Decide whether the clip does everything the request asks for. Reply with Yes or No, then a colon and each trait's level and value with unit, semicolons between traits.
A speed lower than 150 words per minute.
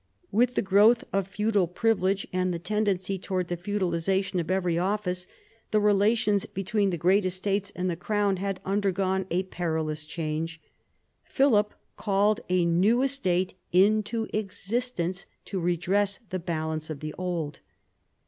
Yes: average, 140 wpm